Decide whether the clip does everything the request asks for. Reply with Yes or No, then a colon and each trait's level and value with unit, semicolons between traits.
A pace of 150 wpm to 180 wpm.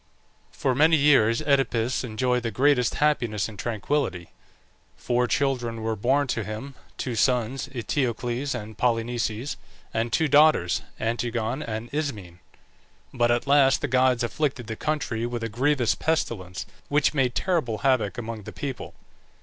No: average, 140 wpm